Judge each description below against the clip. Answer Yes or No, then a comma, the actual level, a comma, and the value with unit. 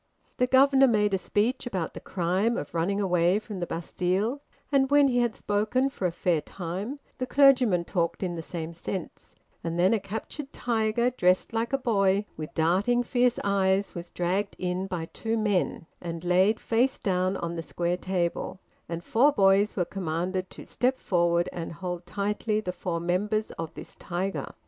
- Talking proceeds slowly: No, average, 180 wpm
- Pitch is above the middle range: Yes, high, 195 Hz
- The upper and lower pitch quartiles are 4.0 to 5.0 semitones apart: Yes, average, 4.5 semitones